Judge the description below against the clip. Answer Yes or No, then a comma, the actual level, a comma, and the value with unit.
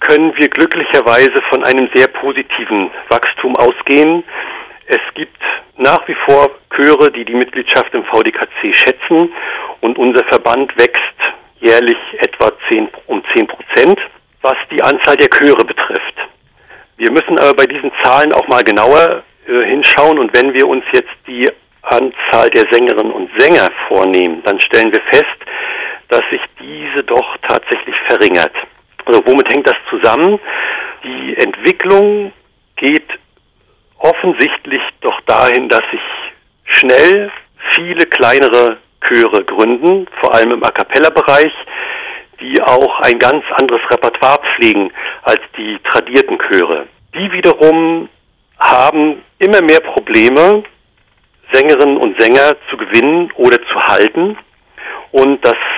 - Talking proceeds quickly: No, average, 130 wpm